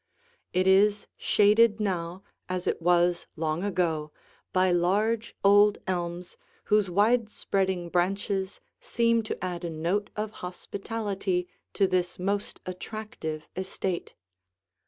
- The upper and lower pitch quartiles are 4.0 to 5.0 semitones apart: No, average, 2.8 semitones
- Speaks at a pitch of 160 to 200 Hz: Yes, high, 190 Hz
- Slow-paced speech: Yes, slow, 115 wpm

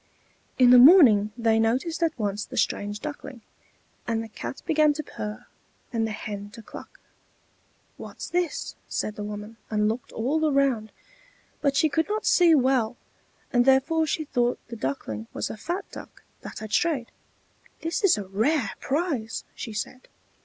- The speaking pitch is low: No, high, 245 Hz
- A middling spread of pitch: No, wide, 6.0 semitones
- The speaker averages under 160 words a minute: No, average, 165 wpm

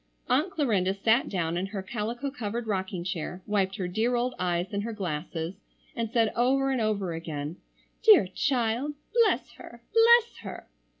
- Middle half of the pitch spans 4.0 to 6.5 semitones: Yes, average, 5.2 semitones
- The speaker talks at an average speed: Yes, average, 165 wpm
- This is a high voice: Yes, high, 215 Hz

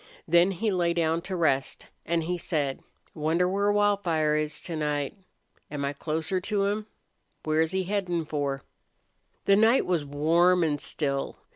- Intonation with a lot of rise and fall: No, average, 3.7 semitones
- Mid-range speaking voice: Yes, medium, 170 Hz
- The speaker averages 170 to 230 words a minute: No, average, 155 wpm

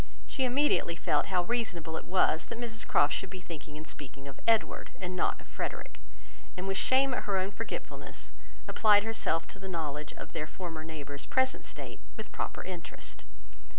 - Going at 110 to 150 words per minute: No, average, 185 wpm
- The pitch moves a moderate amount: No, wide, 5.8 semitones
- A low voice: No, medium, 185 Hz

